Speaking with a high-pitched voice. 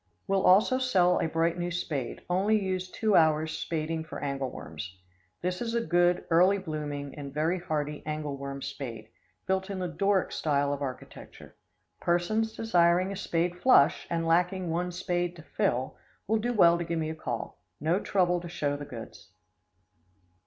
No: medium, 170 Hz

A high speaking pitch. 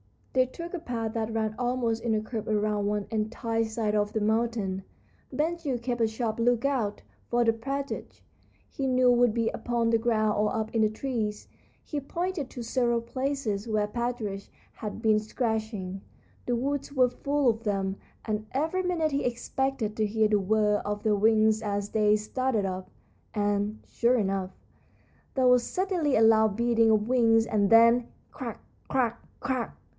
Yes: high, 225 Hz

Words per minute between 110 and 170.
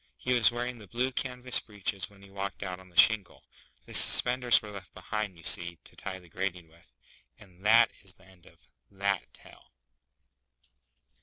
No: average, 180 wpm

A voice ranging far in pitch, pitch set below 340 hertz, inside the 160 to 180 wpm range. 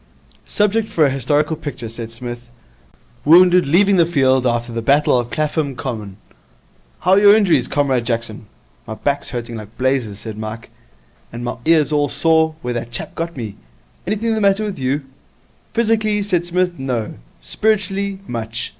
Yes: wide, 7.4 semitones; medium, 140 Hz; average, 165 wpm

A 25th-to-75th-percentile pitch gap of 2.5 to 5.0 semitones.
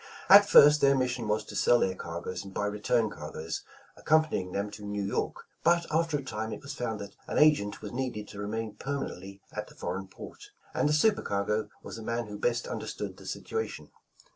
No: wide, 5.5 semitones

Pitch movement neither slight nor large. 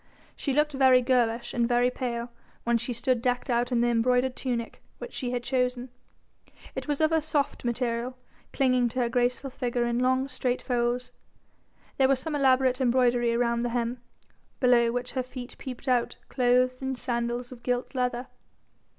No: narrow, 1.3 semitones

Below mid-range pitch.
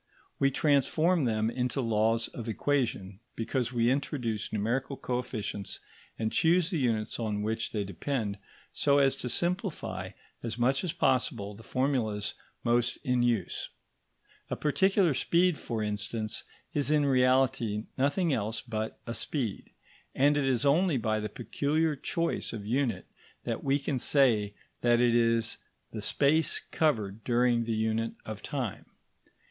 Yes: low, 120 Hz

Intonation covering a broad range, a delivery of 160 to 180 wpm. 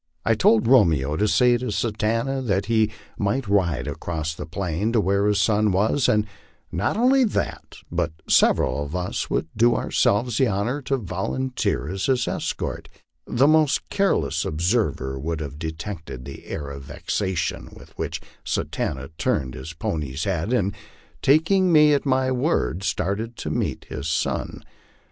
Yes: wide, 7.4 semitones; average, 170 wpm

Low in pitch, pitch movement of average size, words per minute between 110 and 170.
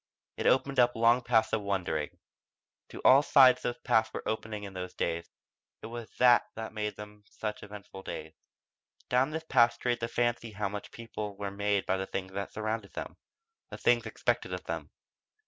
No: low, 110 Hz; average, 3.2 semitones; average, 185 wpm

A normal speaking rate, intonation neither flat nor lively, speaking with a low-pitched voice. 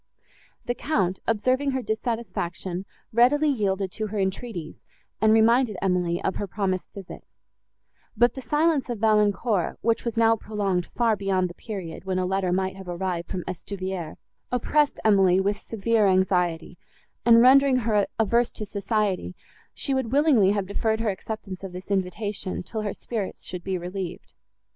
No: average, 160 wpm; average, 3.6 semitones; high, 205 Hz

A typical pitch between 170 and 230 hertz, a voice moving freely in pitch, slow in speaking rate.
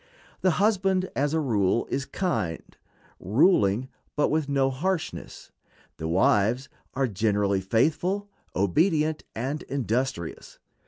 No: low, 135 Hz; wide, 7.6 semitones; slow, 110 wpm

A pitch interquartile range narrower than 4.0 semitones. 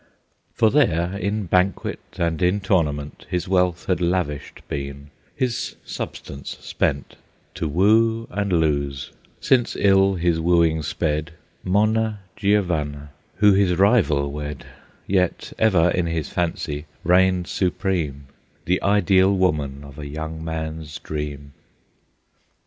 No: average, 4.5 semitones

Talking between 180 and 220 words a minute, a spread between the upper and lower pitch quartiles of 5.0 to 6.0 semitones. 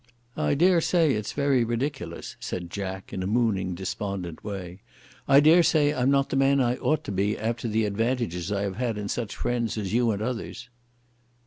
Yes: average, 195 wpm; wide, 5.4 semitones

